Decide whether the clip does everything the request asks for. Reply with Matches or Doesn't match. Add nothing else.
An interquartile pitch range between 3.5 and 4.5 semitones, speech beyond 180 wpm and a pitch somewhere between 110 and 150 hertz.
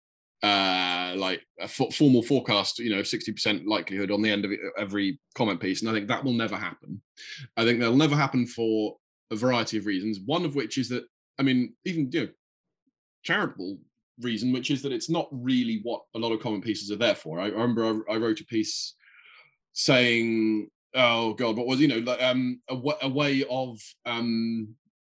Doesn't match